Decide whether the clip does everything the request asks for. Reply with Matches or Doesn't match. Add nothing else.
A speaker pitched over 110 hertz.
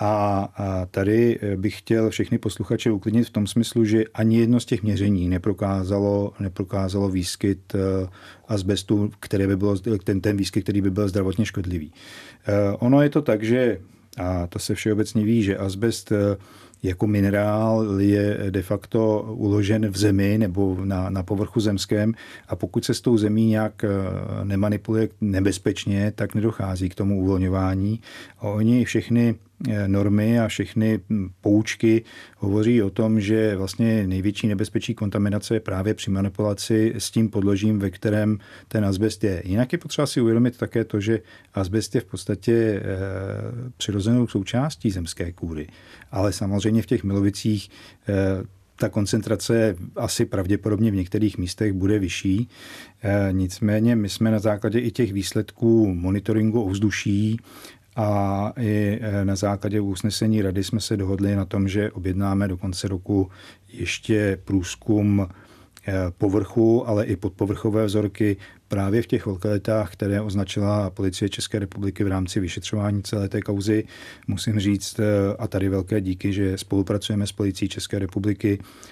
Doesn't match